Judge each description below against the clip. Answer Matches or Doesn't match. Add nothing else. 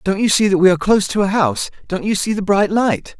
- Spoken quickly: Matches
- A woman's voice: Doesn't match